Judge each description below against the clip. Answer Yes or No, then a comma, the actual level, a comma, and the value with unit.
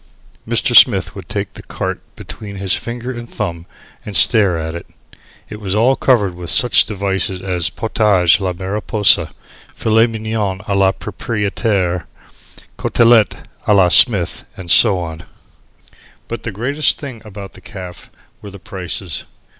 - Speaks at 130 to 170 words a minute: Yes, average, 145 wpm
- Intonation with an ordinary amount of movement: Yes, average, 3.4 semitones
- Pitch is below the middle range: Yes, low, 100 Hz